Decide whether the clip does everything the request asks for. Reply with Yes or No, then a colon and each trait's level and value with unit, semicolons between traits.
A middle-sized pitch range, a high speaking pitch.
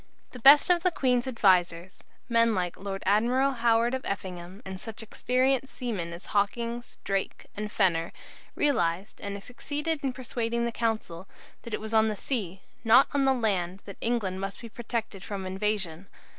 Yes: average, 4.2 semitones; high, 220 Hz